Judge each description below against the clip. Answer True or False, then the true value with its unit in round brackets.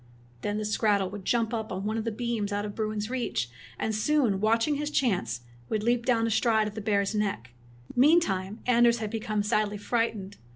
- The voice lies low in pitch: False (215 Hz)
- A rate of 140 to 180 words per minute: False (200 wpm)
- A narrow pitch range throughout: True (2.2 semitones)